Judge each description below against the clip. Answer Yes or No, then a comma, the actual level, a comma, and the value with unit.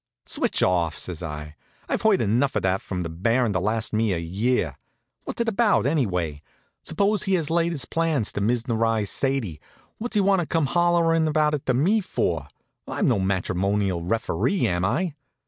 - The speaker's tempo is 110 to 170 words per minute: No, average, 185 wpm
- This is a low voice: Yes, low, 115 Hz